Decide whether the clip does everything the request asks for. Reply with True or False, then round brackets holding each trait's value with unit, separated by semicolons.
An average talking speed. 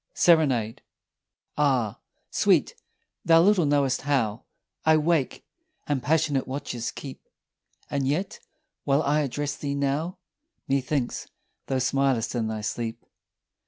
False (115 wpm)